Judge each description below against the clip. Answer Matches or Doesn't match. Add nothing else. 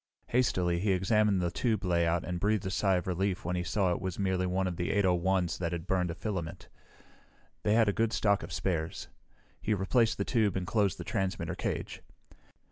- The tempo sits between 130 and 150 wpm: Doesn't match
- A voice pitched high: Doesn't match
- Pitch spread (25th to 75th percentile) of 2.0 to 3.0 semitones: Matches